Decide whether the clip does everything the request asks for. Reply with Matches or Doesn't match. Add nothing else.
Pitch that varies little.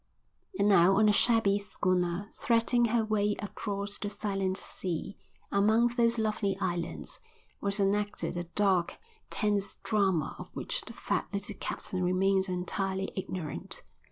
Matches